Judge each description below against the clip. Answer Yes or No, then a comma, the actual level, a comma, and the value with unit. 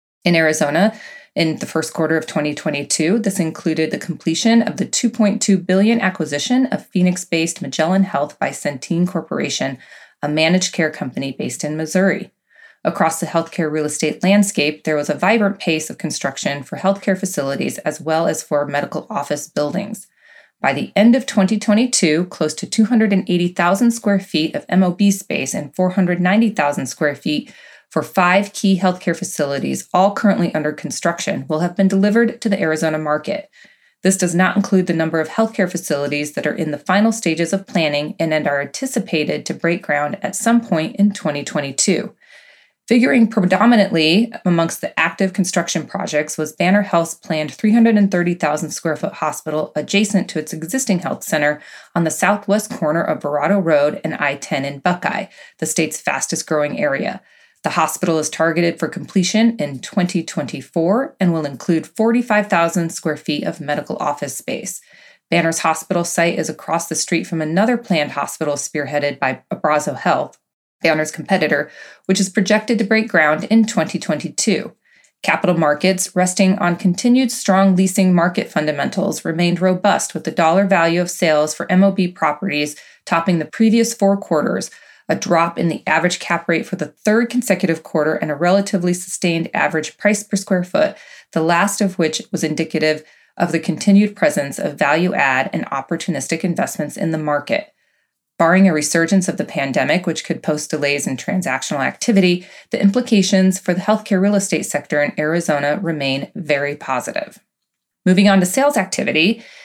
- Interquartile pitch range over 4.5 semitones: No, average, 4.2 semitones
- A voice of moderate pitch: Yes, medium, 175 Hz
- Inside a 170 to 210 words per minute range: No, average, 160 wpm